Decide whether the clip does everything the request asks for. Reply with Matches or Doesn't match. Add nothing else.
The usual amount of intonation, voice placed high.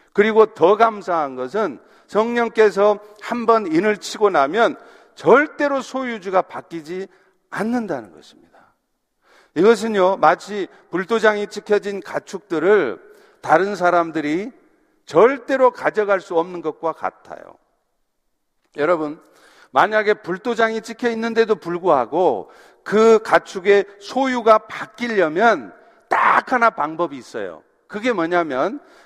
Matches